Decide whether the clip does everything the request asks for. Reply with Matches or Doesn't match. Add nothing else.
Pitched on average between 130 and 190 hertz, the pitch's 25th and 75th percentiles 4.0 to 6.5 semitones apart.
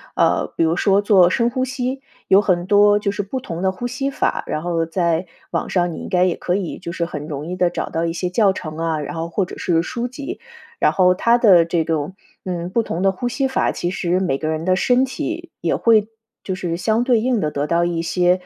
Matches